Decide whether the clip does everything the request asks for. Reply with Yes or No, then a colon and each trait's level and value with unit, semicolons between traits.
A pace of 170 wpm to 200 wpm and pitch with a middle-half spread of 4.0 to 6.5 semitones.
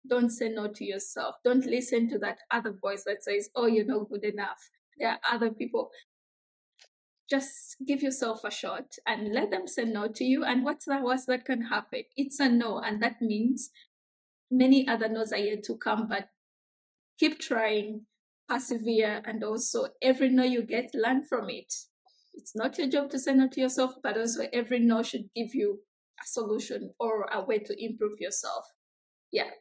No: average, 190 wpm; average, 3.4 semitones